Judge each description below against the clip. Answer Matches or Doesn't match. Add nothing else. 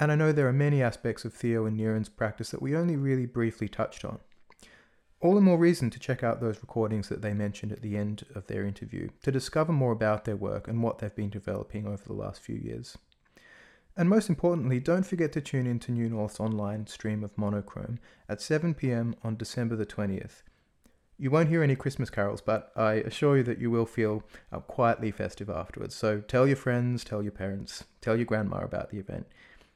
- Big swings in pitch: Doesn't match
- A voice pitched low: Matches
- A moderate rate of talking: Doesn't match